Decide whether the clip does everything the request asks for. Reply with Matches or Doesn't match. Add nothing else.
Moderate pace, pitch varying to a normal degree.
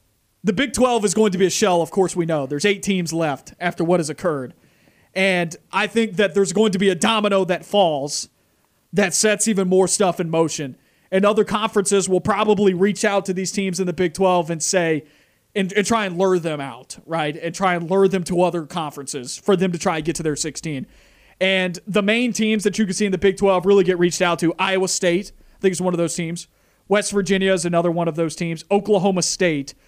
Doesn't match